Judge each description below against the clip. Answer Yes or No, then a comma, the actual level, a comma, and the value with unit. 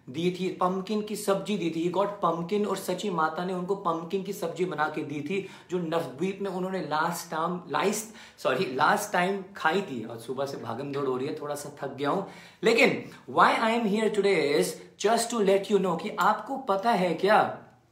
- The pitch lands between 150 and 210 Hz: Yes, medium, 185 Hz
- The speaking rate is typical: No, fast, 210 wpm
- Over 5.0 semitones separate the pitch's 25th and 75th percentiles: No, average, 3.9 semitones